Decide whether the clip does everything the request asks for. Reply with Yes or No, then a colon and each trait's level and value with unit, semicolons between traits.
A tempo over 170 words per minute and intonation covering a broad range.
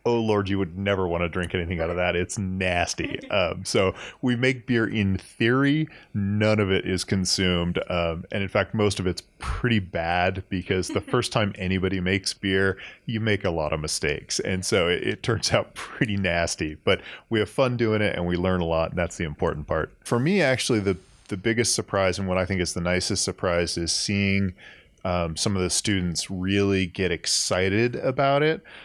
No: fast, 205 wpm; average, 2.9 semitones